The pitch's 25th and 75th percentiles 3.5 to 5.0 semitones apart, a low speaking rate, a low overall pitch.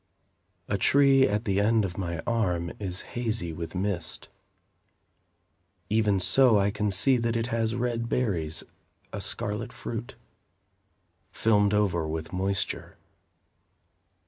Yes: average, 4.3 semitones; slow, 120 wpm; low, 105 Hz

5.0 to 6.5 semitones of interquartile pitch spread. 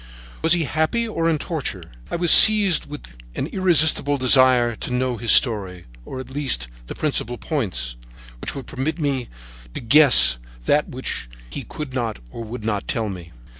Yes: wide, 5.5 semitones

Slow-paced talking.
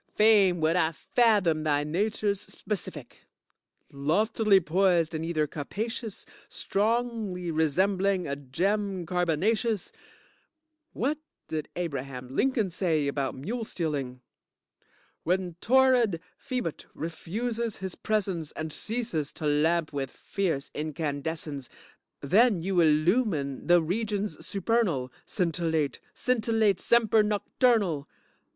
Yes: slow, 100 wpm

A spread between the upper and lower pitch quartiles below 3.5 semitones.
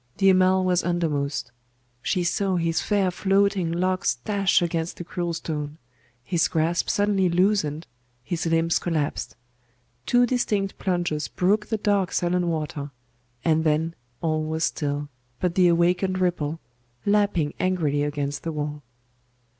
Yes: average, 3.1 semitones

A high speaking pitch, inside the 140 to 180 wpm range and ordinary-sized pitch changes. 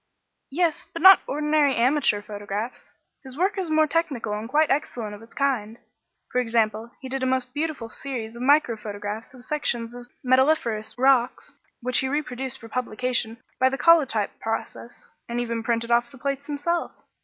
Yes: very high, 250 Hz; average, 170 wpm; average, 4.0 semitones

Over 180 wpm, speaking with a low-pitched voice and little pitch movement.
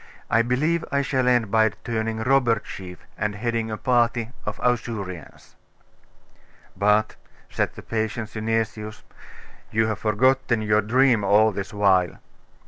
No: slow, 135 wpm; low, 110 Hz; narrow, 2.3 semitones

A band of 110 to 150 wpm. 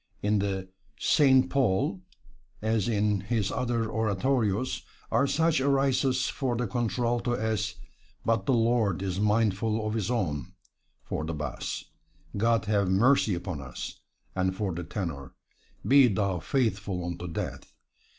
Yes: slow, 135 wpm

